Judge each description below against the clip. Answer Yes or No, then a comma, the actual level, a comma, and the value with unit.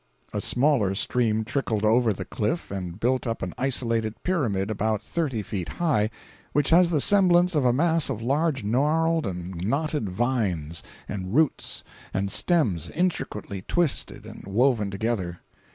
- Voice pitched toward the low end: Yes, low, 115 Hz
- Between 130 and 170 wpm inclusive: Yes, average, 150 wpm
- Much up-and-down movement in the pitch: Yes, wide, 7.0 semitones